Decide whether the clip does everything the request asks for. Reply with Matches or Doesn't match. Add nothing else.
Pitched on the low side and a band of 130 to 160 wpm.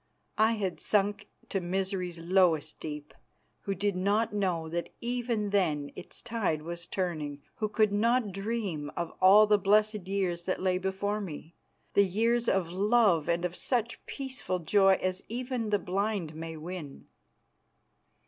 Doesn't match